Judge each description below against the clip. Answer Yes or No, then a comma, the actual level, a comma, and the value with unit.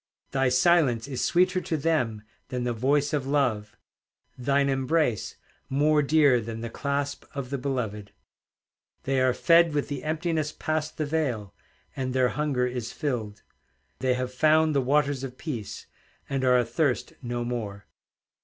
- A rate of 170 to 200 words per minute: No, average, 155 wpm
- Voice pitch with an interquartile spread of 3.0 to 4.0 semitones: Yes, average, 3.3 semitones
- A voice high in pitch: No, low, 135 Hz